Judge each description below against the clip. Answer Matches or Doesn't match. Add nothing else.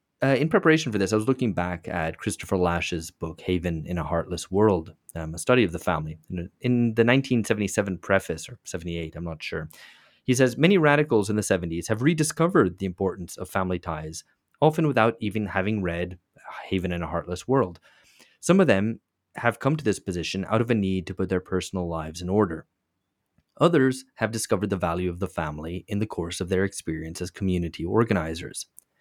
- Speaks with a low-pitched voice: Matches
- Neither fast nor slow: Matches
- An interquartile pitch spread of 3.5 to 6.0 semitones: Matches